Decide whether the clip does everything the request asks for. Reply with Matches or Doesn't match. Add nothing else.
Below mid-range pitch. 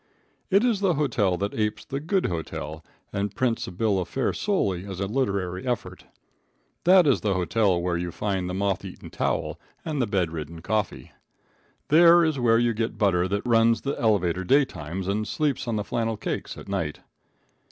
Matches